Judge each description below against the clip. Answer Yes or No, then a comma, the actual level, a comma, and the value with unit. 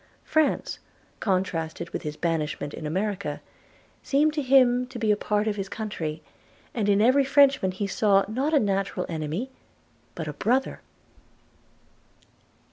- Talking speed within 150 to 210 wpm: No, average, 140 wpm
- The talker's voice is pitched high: Yes, high, 205 Hz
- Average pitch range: No, wide, 6.8 semitones